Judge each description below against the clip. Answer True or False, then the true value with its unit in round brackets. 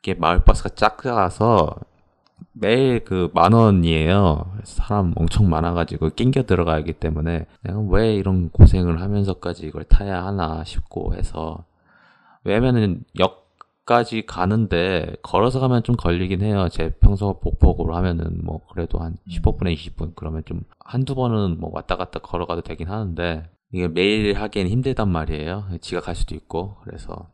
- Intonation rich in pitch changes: False (3.7 semitones)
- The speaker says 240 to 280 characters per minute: False (320 characters per minute)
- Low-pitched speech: True (90 Hz)